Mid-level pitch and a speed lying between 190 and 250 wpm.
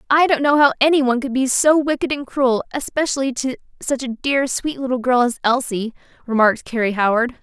No: very high, 260 Hz; average, 200 wpm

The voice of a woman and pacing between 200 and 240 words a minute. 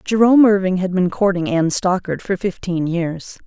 No: female; average, 175 wpm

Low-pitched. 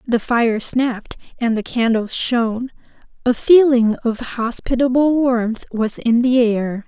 No: high, 240 Hz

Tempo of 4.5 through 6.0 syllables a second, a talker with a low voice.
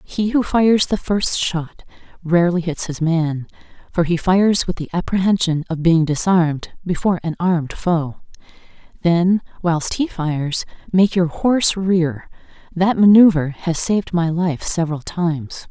No: 4.6 syllables/s; medium, 175 Hz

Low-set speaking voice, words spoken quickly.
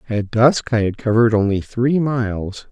No: low, 115 Hz; average, 175 wpm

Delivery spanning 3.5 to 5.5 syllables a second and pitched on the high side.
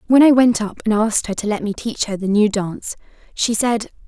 No: 5.7 syllables/s; high, 215 Hz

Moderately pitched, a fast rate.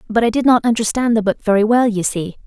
No: high, 220 Hz; fast, 270 wpm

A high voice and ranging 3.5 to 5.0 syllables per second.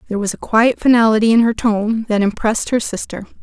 No: high, 220 Hz; 6.2 syllables/s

